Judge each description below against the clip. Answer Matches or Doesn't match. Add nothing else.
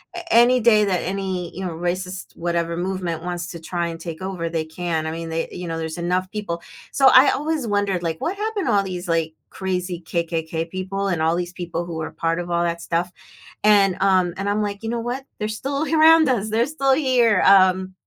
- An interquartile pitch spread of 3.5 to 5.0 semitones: Matches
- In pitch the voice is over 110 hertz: Matches